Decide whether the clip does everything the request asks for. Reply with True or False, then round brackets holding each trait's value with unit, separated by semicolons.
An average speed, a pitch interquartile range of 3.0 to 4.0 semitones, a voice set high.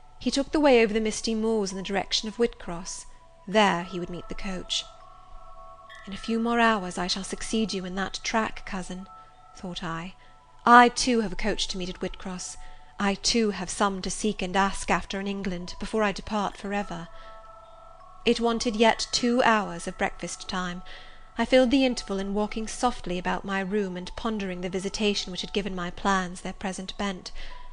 True (190 wpm; 3.3 semitones; 200 Hz)